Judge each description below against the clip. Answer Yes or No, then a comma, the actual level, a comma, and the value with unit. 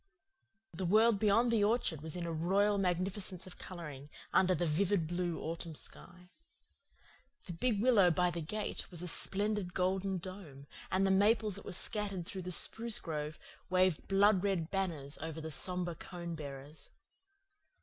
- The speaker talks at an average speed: Yes, average, 160 wpm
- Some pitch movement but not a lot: Yes, average, 3.2 semitones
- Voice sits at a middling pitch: Yes, medium, 180 Hz